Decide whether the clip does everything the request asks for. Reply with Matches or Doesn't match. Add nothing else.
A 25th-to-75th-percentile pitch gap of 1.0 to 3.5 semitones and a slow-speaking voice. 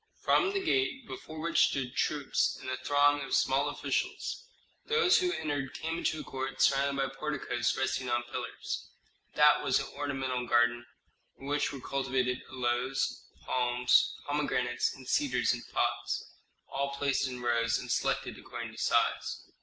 Doesn't match